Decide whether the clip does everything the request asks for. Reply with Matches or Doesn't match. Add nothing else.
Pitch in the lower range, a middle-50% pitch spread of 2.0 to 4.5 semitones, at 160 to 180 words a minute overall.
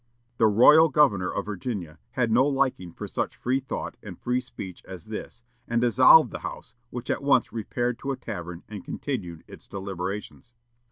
Doesn't match